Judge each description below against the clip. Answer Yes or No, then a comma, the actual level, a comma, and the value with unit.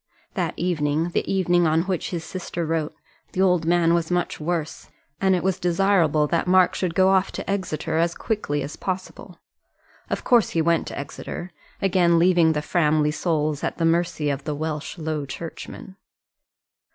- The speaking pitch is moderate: Yes, medium, 170 Hz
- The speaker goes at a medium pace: Yes, average, 175 wpm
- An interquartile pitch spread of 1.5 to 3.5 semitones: Yes, narrow, 2.6 semitones